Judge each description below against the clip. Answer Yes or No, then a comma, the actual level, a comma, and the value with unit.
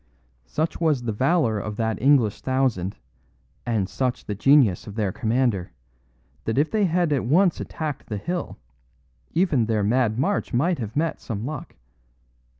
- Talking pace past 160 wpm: No, average, 155 wpm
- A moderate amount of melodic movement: No, wide, 6.0 semitones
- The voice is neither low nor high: No, low, 125 Hz